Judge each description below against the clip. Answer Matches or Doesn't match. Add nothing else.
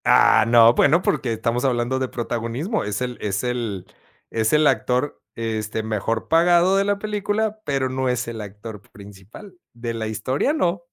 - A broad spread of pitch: Matches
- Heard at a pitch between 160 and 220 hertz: Doesn't match